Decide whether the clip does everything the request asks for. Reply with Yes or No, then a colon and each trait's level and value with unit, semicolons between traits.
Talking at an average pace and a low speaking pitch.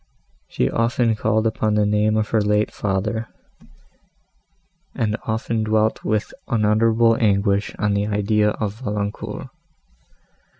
No: slow, 120 wpm; low, 105 Hz